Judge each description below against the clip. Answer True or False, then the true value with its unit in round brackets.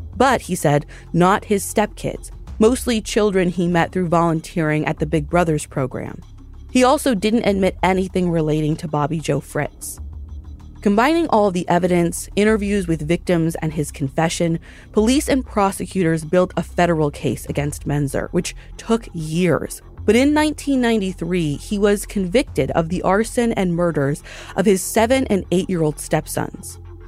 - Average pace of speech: True (150 wpm)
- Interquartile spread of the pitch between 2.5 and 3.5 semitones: False (4.7 semitones)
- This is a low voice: False (175 Hz)